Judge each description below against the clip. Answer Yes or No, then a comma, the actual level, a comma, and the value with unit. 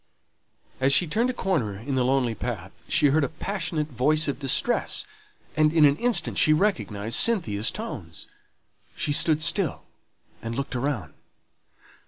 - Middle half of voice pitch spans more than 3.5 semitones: Yes, average, 5.3 semitones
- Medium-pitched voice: Yes, medium, 145 Hz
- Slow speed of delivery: No, average, 150 wpm